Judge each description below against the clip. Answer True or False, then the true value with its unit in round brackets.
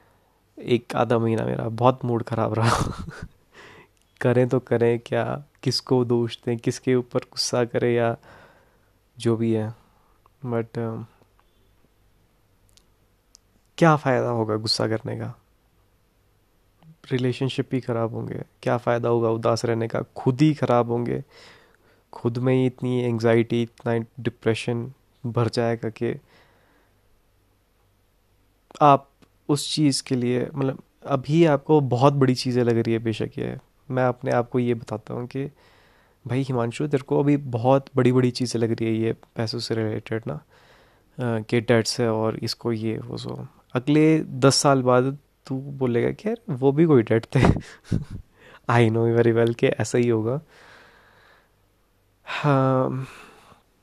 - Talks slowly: False (140 wpm)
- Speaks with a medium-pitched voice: False (120 Hz)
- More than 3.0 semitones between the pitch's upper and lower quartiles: False (2.6 semitones)